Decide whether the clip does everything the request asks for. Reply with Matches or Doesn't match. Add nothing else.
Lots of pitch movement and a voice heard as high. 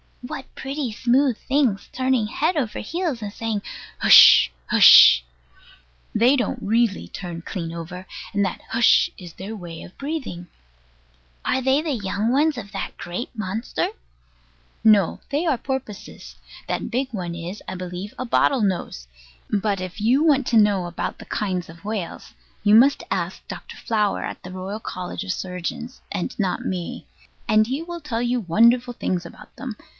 Matches